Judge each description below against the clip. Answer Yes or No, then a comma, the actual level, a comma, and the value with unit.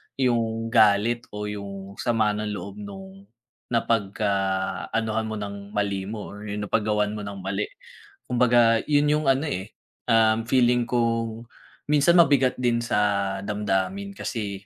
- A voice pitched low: Yes, low, 110 Hz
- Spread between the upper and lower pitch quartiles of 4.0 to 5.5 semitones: No, average, 2.8 semitones